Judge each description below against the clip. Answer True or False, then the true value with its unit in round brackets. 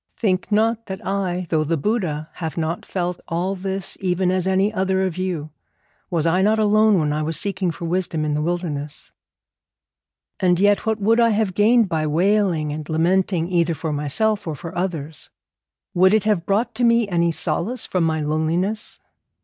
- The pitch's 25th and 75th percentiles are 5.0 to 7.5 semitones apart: False (4.0 semitones)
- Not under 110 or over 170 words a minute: False (180 wpm)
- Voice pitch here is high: False (180 Hz)